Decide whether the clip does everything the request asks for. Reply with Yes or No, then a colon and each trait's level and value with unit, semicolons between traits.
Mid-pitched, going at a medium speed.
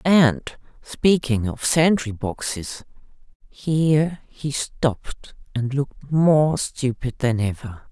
No: medium, 145 Hz; slow, 100 wpm